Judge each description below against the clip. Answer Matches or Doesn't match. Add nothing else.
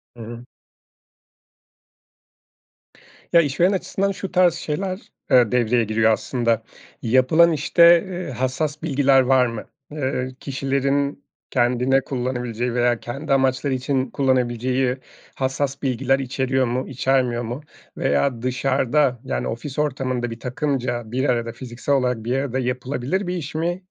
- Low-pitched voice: Matches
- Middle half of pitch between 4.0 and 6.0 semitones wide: Doesn't match